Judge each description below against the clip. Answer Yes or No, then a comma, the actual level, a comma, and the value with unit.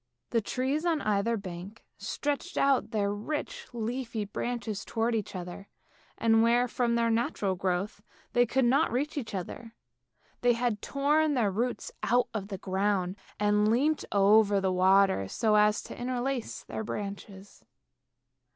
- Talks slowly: No, average, 150 wpm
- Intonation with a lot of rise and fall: No, average, 3.6 semitones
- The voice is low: No, high, 225 Hz